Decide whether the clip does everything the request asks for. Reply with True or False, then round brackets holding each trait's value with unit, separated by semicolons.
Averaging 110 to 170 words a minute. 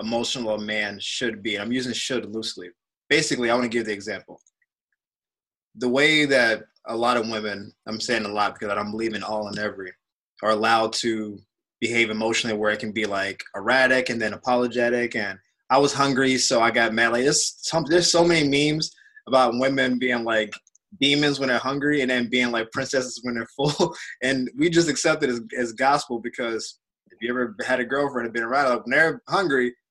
False (200 wpm)